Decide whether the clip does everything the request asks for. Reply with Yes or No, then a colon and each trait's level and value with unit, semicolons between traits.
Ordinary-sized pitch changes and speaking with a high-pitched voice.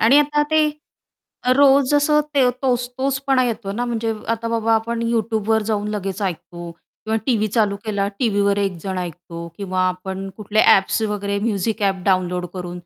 Yes: average, 3.4 semitones; high, 215 Hz